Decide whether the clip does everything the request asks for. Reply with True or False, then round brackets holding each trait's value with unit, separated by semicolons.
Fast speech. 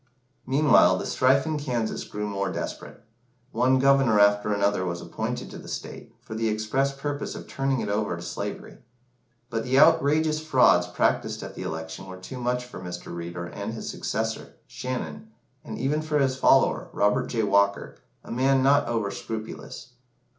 False (170 wpm)